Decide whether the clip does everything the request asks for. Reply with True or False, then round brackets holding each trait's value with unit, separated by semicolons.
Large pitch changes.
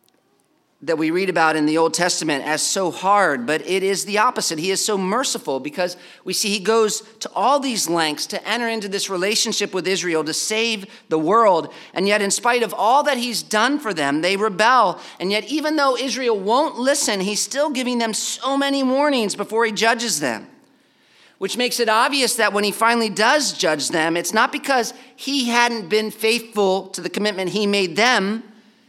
False (4.2 semitones)